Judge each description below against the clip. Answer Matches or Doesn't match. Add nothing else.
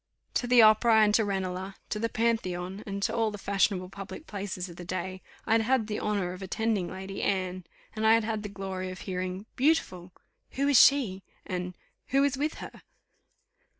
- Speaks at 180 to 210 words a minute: Matches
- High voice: Matches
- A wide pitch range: Doesn't match